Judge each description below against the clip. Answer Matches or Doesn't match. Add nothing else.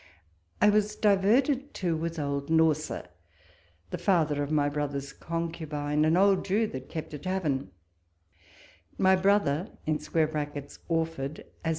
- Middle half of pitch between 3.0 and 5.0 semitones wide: Matches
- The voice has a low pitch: Doesn't match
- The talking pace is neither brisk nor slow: Doesn't match